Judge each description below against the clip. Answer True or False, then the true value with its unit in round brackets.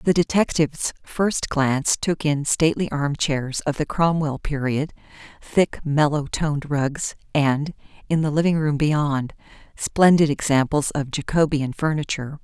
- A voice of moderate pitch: True (150 Hz)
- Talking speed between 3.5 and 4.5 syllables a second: True (4.3 syllables/s)